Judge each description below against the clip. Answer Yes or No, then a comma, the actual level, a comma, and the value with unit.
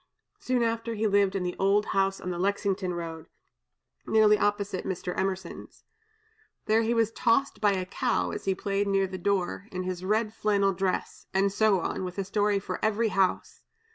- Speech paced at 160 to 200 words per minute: Yes, average, 185 wpm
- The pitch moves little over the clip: Yes, narrow, 2.2 semitones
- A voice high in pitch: Yes, high, 195 Hz